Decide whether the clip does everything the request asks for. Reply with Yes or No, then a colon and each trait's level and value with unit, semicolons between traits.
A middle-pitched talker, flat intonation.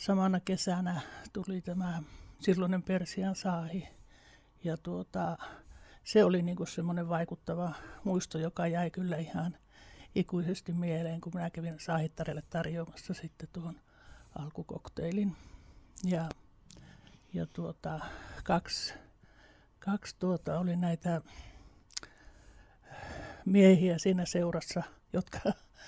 Yes: medium, 170 Hz; narrow, 2.1 semitones